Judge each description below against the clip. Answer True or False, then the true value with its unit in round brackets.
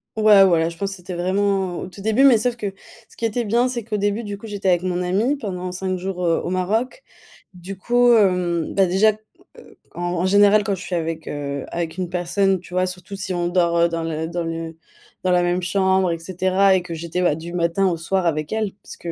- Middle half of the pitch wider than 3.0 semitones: False (2.7 semitones)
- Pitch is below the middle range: False (185 Hz)